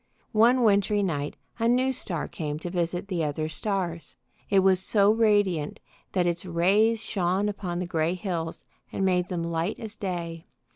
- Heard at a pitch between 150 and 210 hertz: Yes, medium, 185 Hz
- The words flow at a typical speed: Yes, average, 165 wpm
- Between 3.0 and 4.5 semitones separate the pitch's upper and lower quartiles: Yes, average, 3.6 semitones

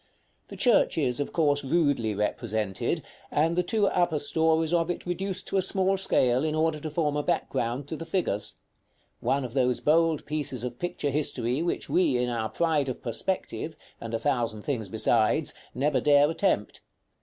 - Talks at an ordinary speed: Yes, average, 180 wpm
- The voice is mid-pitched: Yes, medium, 145 Hz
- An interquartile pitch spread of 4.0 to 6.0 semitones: Yes, average, 5.1 semitones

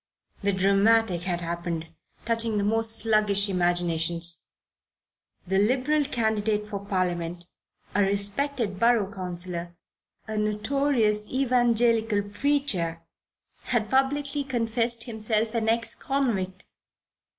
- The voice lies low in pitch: No, high, 210 Hz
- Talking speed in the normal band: No, slow, 100 wpm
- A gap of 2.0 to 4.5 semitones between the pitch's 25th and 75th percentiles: Yes, average, 4.0 semitones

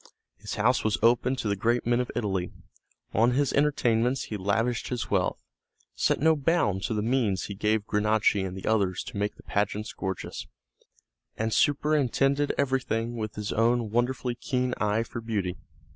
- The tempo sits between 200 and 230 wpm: No, average, 170 wpm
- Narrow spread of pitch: No, average, 3.3 semitones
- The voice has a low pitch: Yes, low, 115 Hz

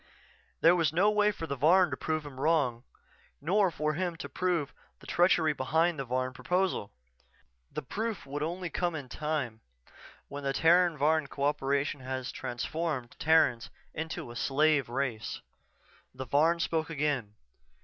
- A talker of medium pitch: Yes, medium, 150 Hz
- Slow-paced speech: No, average, 160 wpm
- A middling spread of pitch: Yes, average, 4.0 semitones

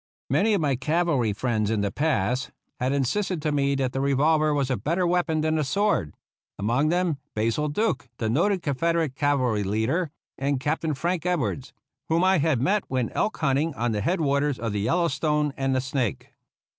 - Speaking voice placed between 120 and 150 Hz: Yes, medium, 140 Hz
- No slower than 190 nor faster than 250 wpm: Yes, average, 195 wpm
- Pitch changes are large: No, average, 4.5 semitones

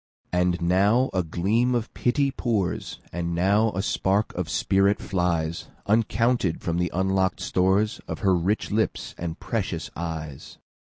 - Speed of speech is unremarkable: No, slow, 125 wpm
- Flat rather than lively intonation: No, average, 3.8 semitones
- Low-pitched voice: Yes, very low, 95 Hz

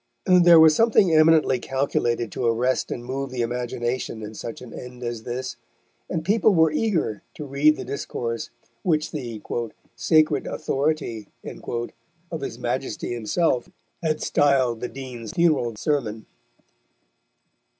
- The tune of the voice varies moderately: Yes, average, 4.7 semitones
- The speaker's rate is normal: No, slow, 130 wpm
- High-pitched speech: No, low, 130 Hz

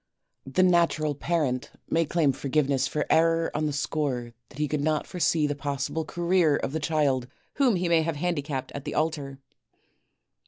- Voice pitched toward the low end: No, medium, 150 Hz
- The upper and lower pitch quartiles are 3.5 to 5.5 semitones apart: No, average, 2.9 semitones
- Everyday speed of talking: Yes, average, 170 wpm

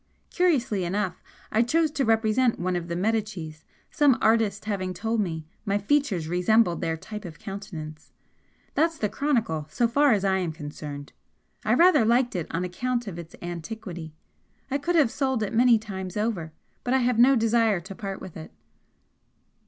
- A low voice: No, high, 210 Hz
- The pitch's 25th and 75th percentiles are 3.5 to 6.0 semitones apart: Yes, wide, 5.4 semitones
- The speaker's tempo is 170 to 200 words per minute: Yes, average, 175 wpm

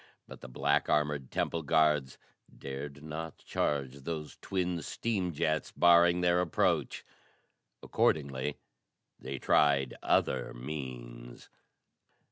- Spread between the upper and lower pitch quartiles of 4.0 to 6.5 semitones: No, average, 3.5 semitones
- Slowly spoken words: Yes, slow, 100 wpm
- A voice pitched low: Yes, very low, 75 Hz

